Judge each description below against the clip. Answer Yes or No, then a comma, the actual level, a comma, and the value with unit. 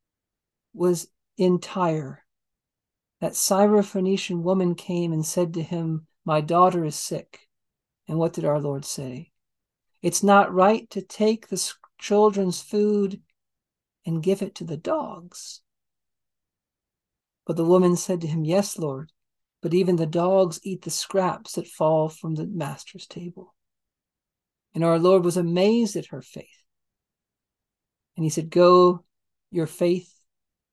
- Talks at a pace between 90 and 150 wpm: Yes, slow, 135 wpm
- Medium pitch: Yes, medium, 175 Hz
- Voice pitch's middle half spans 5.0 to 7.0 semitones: No, average, 2.9 semitones